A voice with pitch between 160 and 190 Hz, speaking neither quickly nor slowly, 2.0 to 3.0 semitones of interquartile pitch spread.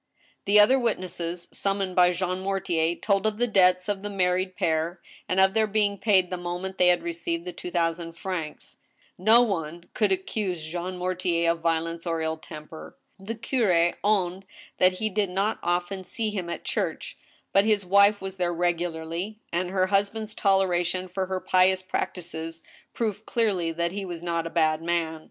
Yes: medium, 185 Hz; average, 180 wpm; narrow, 2.5 semitones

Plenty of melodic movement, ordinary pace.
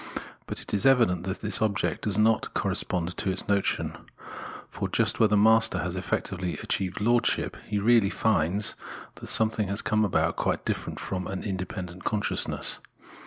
No: average, 2.9 semitones; average, 165 wpm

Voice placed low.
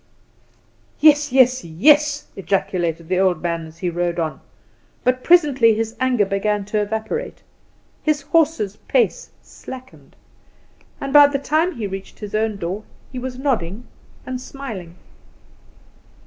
No: high, 225 Hz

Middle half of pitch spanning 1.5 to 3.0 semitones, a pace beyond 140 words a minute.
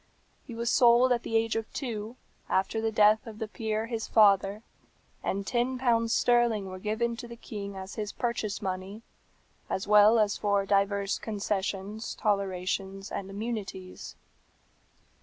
Yes: narrow, 2.6 semitones; average, 150 wpm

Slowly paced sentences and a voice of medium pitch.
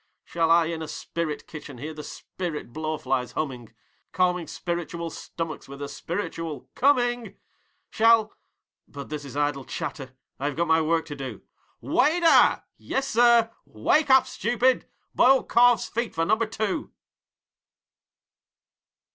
Yes: slow, 130 wpm; medium, 165 Hz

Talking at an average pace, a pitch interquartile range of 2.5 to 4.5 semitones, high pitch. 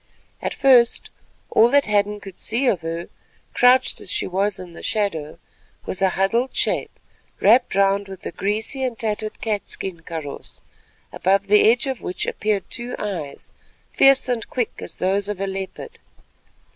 Yes: average, 160 wpm; average, 3.8 semitones; high, 205 Hz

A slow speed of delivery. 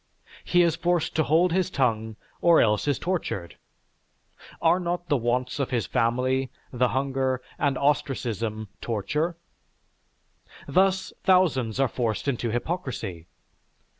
Yes: slow, 125 wpm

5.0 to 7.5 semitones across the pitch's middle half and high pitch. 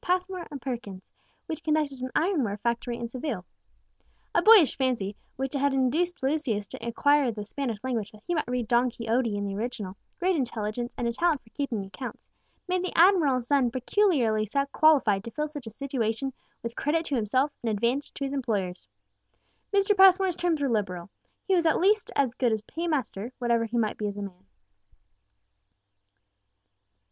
Yes: wide, 5.5 semitones; very high, 255 Hz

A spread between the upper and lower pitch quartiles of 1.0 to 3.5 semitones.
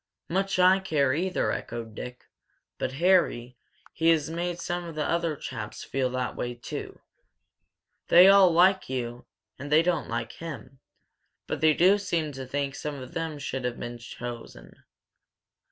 No: wide, 5.5 semitones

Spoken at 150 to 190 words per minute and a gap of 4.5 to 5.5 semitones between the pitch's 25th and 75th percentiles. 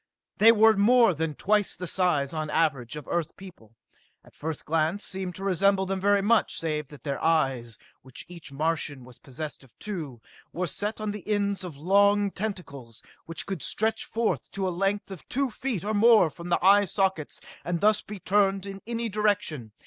No: average, 200 wpm; average, 4.9 semitones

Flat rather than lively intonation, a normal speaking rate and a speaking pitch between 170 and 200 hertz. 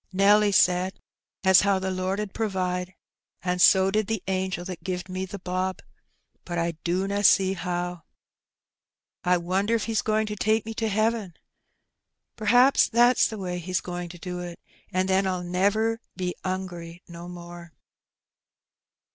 Yes: narrow, 2.3 semitones; average, 160 wpm; medium, 185 Hz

